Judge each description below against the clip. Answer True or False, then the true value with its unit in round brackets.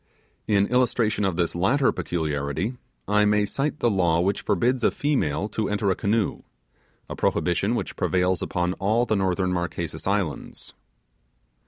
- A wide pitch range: False (3.8 semitones)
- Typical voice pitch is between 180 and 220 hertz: False (100 Hz)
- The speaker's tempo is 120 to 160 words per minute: True (150 wpm)